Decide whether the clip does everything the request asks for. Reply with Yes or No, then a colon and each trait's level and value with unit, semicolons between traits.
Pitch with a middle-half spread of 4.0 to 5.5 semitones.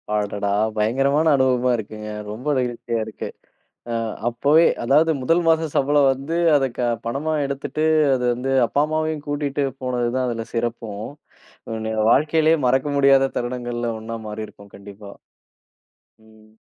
Yes: average, 4.4 semitones